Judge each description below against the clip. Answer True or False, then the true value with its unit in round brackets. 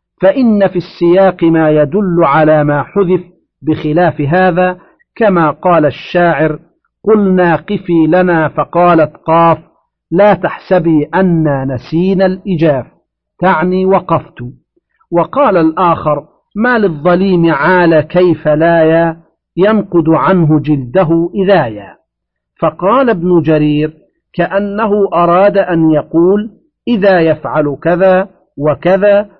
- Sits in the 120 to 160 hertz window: False (175 Hz)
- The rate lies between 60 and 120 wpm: True (95 wpm)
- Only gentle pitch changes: False (3.3 semitones)